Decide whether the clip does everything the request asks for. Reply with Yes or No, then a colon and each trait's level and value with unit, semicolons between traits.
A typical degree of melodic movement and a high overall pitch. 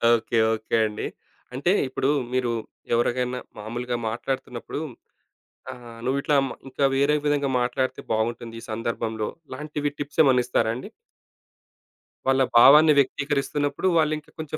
No: average, 3.5 semitones; low, 130 Hz